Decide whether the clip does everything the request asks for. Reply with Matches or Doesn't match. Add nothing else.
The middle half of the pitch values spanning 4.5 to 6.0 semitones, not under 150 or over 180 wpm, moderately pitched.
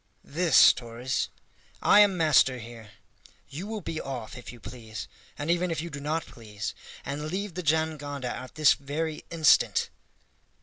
Matches